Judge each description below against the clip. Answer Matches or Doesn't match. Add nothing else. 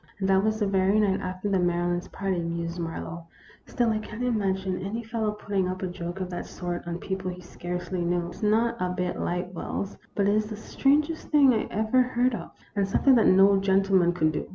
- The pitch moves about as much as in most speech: Matches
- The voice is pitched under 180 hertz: Doesn't match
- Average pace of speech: Doesn't match